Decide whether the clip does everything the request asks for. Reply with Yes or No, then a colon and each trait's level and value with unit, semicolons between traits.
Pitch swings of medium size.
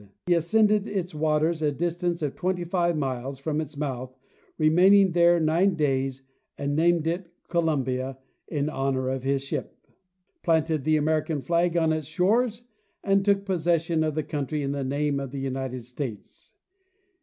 Yes: average, 3.9 semitones